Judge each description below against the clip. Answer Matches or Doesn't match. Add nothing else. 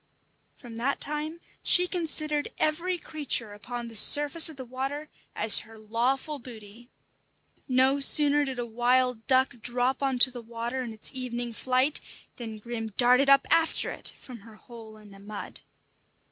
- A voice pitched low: Doesn't match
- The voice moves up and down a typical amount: Matches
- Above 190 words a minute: Doesn't match